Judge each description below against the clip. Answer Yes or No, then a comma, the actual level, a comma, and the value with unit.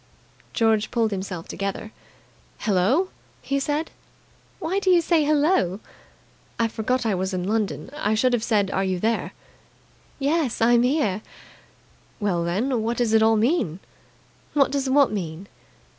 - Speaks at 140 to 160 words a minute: Yes, average, 145 wpm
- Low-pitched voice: No, high, 225 Hz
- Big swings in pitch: Yes, wide, 5.8 semitones